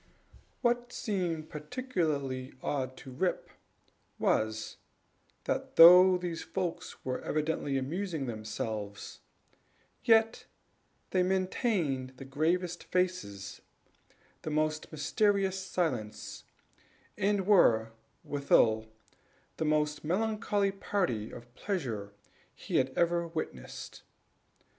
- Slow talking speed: Yes, slow, 90 wpm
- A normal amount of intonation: No, wide, 6.4 semitones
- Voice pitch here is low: No, medium, 160 Hz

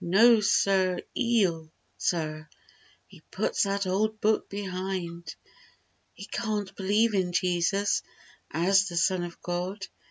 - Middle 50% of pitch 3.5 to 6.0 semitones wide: No, narrow, 2.6 semitones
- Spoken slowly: Yes, slow, 120 wpm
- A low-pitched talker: No, high, 190 Hz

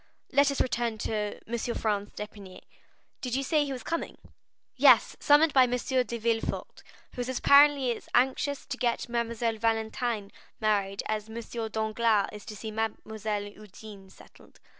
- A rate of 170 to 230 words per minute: No, average, 155 wpm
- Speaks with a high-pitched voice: Yes, high, 225 Hz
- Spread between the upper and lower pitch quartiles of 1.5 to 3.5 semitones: Yes, average, 2.9 semitones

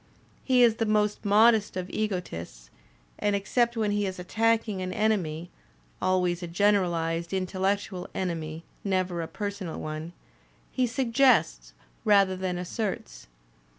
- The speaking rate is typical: No, slow, 125 wpm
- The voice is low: No, high, 190 Hz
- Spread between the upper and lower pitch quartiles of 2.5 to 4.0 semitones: Yes, average, 3.7 semitones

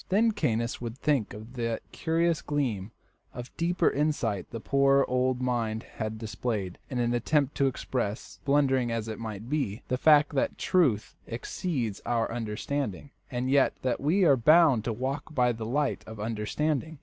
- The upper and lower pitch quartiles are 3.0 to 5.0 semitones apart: Yes, average, 4.6 semitones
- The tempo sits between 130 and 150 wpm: No, average, 165 wpm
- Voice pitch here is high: No, low, 125 Hz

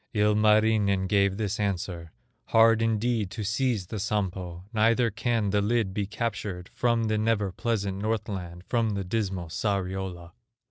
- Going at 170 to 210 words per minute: No, average, 140 wpm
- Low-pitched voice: Yes, low, 105 Hz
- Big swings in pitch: No, average, 2.8 semitones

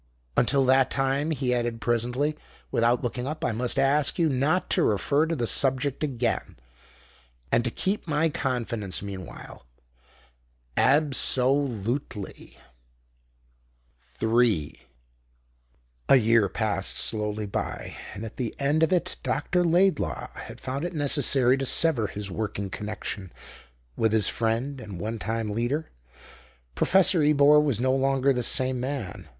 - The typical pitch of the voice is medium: No, low, 125 Hz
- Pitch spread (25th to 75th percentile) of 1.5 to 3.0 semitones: No, average, 4.2 semitones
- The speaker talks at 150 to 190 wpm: No, average, 140 wpm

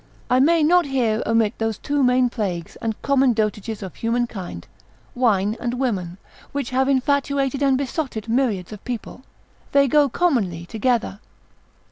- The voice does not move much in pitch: No, average, 4.2 semitones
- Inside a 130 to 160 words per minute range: Yes, average, 150 wpm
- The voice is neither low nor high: No, high, 245 Hz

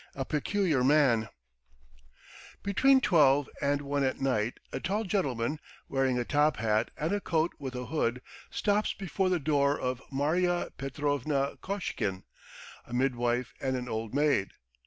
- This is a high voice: No, medium, 140 Hz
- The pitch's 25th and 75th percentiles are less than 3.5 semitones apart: No, average, 4.2 semitones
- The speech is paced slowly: No, average, 145 wpm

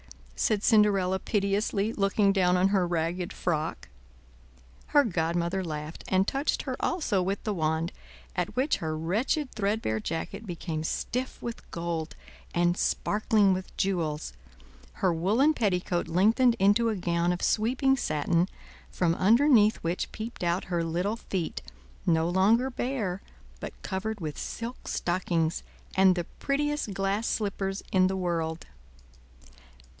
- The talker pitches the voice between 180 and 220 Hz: Yes, high, 190 Hz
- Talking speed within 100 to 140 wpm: Yes, slow, 135 wpm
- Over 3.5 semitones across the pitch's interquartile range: Yes, average, 4.1 semitones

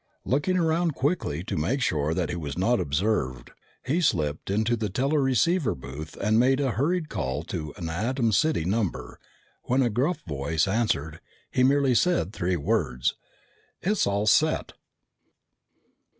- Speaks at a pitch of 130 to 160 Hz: No, low, 110 Hz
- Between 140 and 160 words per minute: Yes, average, 150 wpm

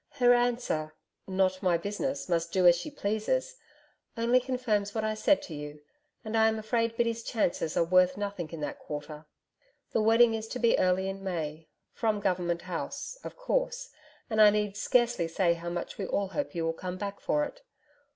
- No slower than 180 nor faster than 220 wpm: Yes, average, 190 wpm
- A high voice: Yes, high, 205 Hz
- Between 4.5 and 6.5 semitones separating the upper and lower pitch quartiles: Yes, average, 5.1 semitones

